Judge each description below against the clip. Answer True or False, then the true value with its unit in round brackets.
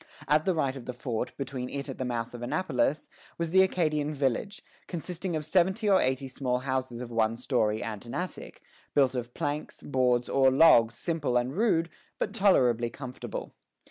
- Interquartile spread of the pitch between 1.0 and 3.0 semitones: False (4.9 semitones)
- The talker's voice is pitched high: False (135 Hz)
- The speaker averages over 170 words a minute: True (185 wpm)